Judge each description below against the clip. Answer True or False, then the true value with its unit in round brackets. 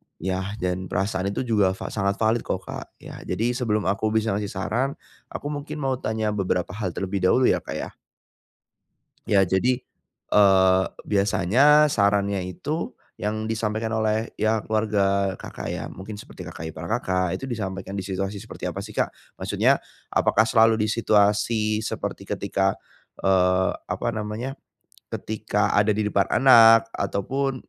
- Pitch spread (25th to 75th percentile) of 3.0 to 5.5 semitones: False (2.6 semitones)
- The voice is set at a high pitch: False (105 Hz)